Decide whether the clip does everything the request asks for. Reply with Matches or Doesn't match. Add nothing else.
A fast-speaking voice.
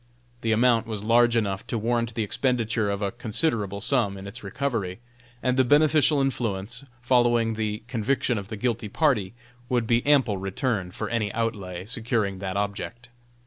Doesn't match